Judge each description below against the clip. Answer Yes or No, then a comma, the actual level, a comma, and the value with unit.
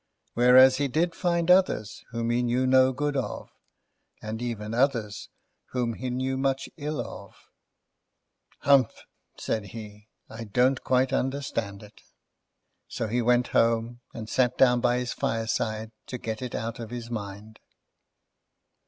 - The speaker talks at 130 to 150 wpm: Yes, average, 145 wpm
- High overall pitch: No, low, 120 Hz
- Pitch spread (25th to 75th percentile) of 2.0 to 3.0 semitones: Yes, average, 2.7 semitones